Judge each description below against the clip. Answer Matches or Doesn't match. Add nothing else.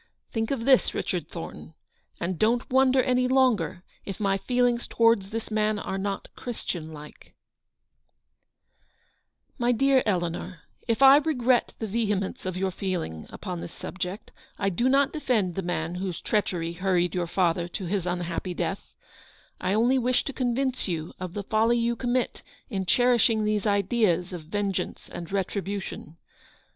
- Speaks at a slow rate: Doesn't match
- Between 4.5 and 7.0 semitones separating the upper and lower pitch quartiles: Matches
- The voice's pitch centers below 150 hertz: Doesn't match